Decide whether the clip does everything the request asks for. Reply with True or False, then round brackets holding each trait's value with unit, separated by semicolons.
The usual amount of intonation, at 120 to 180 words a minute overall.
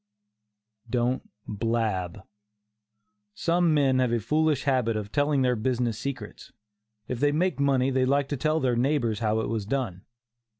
True (3.9 semitones; 155 wpm)